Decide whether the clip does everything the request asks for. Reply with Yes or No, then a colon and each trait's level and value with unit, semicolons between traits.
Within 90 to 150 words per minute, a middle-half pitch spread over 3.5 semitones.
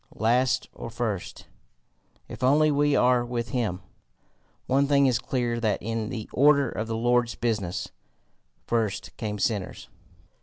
No: average, 140 wpm; narrow, 2.6 semitones